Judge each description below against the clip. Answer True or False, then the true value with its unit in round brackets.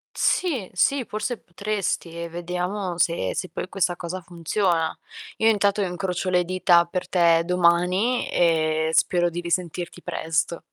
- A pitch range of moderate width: False (2.2 semitones)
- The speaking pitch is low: False (180 Hz)